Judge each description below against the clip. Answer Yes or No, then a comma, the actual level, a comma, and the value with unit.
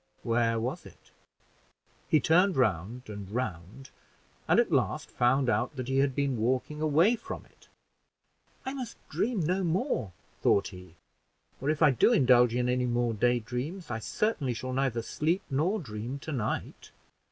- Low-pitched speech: Yes, low, 130 Hz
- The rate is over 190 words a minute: No, average, 160 wpm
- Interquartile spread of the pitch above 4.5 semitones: Yes, average, 5.0 semitones